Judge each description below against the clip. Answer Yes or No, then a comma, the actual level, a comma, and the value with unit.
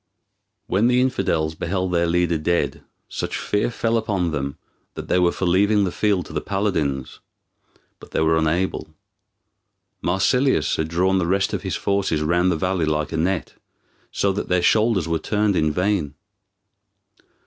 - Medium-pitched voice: No, very low, 90 Hz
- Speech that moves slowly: No, average, 165 wpm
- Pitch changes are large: No, average, 3.7 semitones